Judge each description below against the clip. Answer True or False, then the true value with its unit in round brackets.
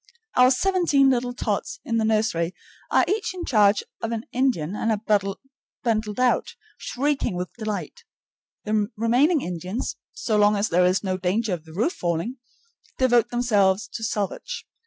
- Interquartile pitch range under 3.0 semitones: False (4.2 semitones)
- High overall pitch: True (220 Hz)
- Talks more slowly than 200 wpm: True (155 wpm)